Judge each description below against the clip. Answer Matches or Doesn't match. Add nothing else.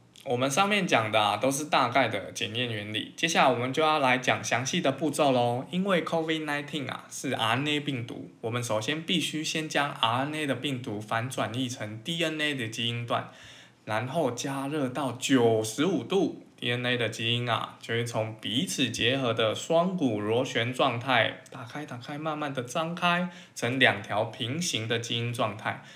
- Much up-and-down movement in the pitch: Doesn't match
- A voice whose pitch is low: Matches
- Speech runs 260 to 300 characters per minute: Matches